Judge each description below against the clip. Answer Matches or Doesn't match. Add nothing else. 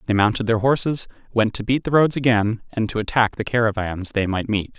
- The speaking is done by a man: Matches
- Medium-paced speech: Doesn't match